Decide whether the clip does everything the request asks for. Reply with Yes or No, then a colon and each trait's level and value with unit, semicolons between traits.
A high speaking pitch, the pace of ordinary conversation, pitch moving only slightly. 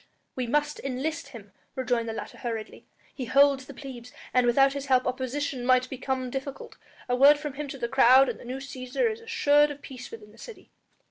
No: very high, 265 Hz; fast, 210 wpm; narrow, 2.2 semitones